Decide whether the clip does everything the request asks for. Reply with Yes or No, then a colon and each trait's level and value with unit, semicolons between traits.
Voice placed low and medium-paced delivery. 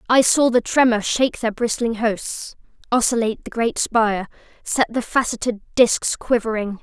No: high, 230 Hz; average, 150 wpm